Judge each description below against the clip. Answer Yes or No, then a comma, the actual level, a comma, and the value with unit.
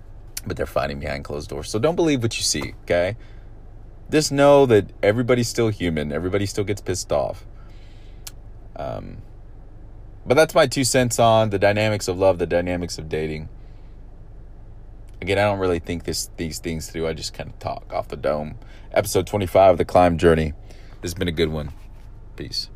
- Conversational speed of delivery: Yes, average, 185 wpm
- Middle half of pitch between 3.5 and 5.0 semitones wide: Yes, average, 3.9 semitones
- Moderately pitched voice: No, low, 105 Hz